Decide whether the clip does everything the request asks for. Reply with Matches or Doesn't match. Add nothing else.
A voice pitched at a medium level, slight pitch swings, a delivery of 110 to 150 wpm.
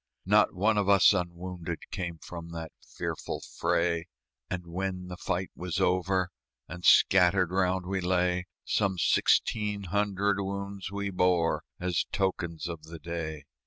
Doesn't match